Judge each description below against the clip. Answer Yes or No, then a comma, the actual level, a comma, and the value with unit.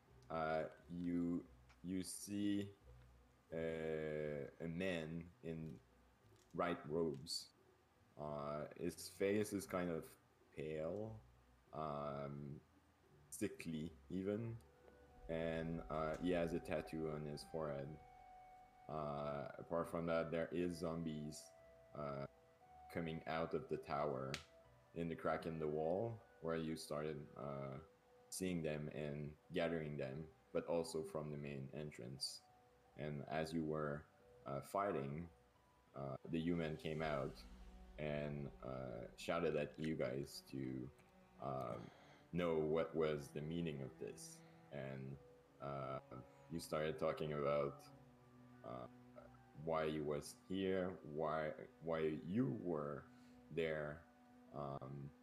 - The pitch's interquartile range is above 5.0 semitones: No, average, 2.8 semitones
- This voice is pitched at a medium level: No, very low, 80 Hz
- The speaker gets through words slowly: Yes, slow, 115 wpm